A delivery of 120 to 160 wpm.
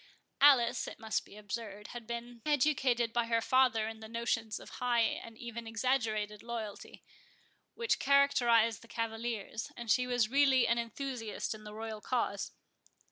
Yes: average, 155 wpm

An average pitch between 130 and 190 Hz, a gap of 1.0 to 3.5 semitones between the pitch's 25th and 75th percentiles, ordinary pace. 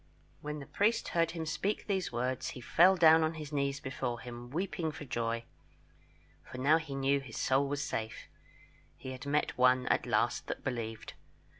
No: medium, 140 Hz; average, 4.1 semitones; average, 180 wpm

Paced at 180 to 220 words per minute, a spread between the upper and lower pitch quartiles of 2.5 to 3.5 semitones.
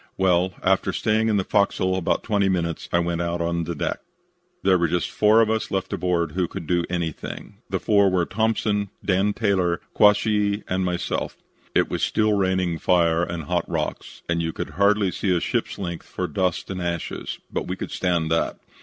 Yes: average, 190 wpm; average, 2.8 semitones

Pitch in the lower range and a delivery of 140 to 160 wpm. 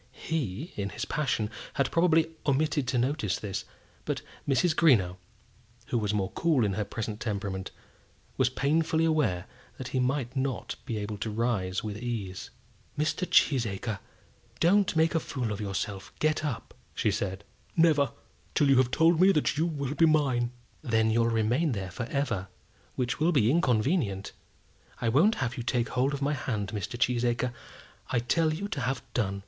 No: low, 125 Hz; average, 170 wpm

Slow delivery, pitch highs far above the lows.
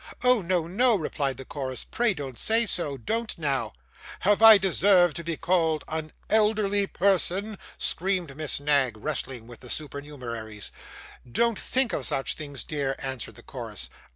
No: average, 155 wpm; wide, 6.8 semitones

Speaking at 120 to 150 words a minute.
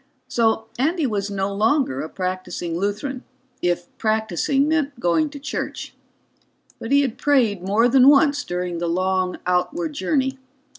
Yes: average, 145 wpm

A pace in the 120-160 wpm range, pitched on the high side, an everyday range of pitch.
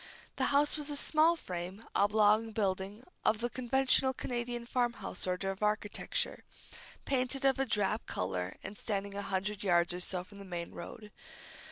No: average, 170 wpm; high, 210 Hz; average, 4.5 semitones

